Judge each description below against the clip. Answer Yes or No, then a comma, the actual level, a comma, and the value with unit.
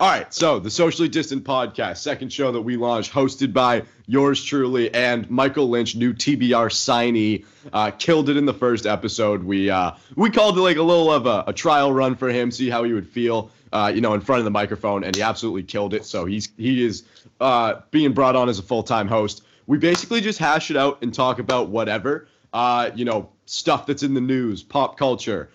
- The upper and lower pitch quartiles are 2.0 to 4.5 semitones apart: Yes, average, 3.8 semitones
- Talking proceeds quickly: Yes, fast, 225 wpm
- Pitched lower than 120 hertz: No, low, 125 Hz